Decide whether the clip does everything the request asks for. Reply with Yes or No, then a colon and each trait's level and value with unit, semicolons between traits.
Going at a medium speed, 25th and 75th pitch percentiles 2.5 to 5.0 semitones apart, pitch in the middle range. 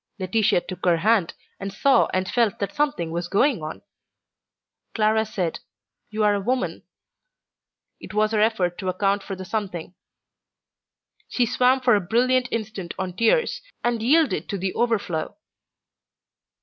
No: average, 150 wpm; average, 4.0 semitones; high, 210 Hz